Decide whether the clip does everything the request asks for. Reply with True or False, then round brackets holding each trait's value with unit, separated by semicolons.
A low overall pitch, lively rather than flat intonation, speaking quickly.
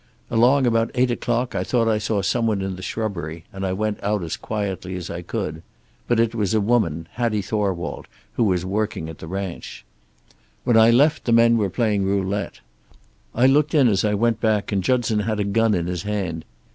False (105 Hz; 3.5 semitones; 210 wpm)